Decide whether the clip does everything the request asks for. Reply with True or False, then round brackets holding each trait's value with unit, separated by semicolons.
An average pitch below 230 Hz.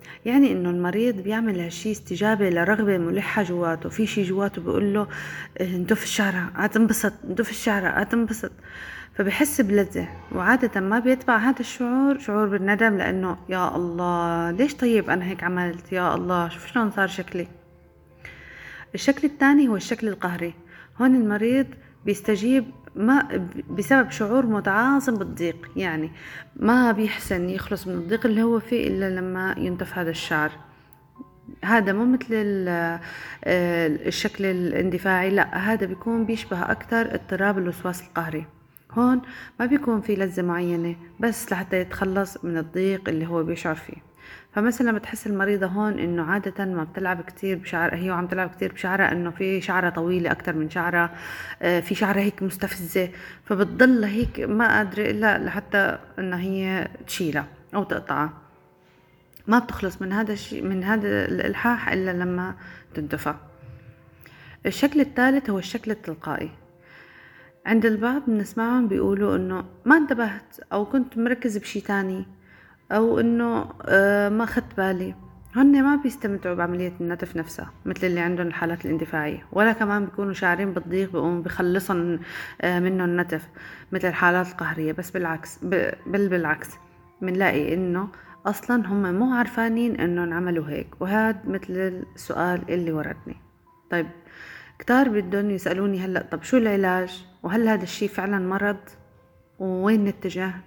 True (190 Hz)